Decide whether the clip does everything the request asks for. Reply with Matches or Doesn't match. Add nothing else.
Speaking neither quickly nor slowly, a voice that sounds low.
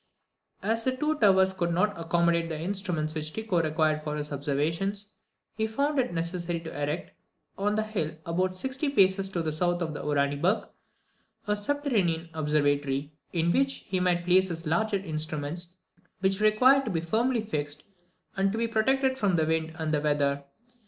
Doesn't match